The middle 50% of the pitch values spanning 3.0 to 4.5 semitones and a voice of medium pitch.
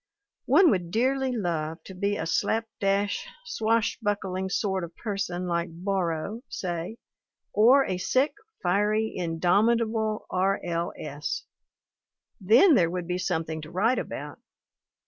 No: average, 4.0 semitones; high, 195 Hz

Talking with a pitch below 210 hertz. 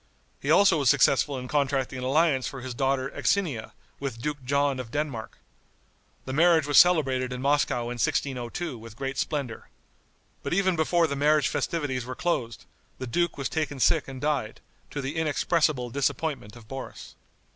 Yes: medium, 140 Hz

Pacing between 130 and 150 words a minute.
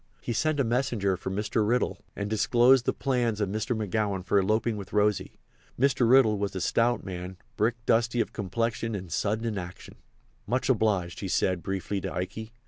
No: average, 185 wpm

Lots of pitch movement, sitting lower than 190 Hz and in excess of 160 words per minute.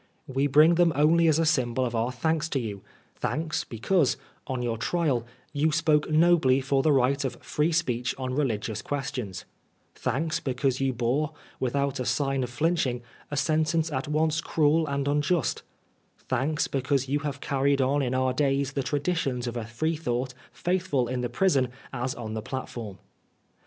No: average, 3.6 semitones; medium, 140 Hz; average, 175 wpm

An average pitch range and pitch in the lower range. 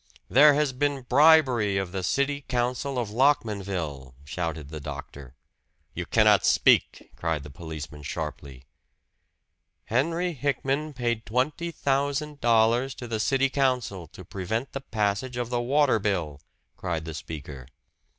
No: wide, 8.5 semitones; low, 120 Hz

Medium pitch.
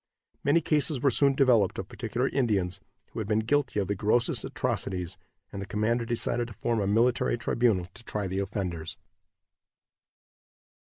No: low, 110 Hz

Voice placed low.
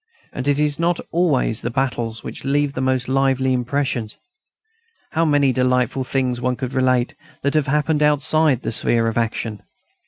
Yes: low, 130 Hz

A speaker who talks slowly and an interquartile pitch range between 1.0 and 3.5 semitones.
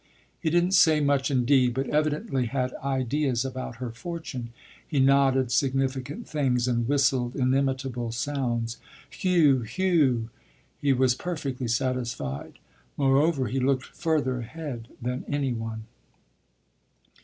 Yes: slow, 120 wpm; average, 2.7 semitones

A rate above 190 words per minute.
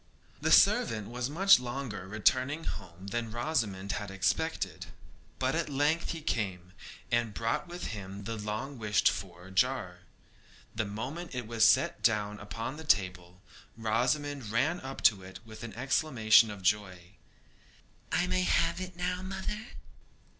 No: average, 145 wpm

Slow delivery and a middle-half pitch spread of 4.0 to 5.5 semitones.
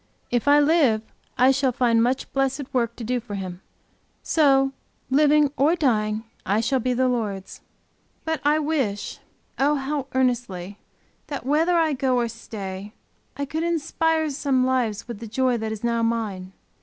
No: average, 165 wpm; average, 4.3 semitones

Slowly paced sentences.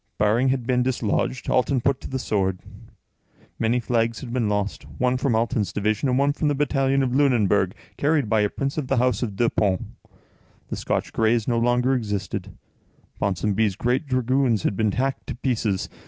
No: average, 185 wpm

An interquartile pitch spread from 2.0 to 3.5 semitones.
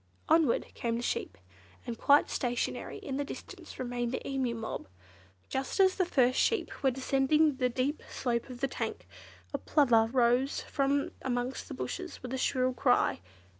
Yes: narrow, 2.4 semitones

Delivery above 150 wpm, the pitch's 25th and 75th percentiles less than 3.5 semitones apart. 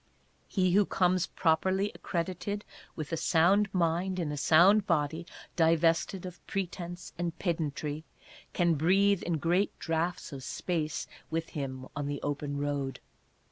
No: average, 140 wpm; average, 3.1 semitones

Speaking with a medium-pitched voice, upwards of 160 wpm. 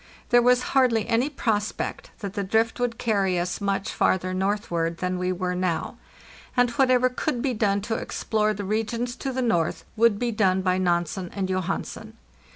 No: high, 210 Hz; average, 175 wpm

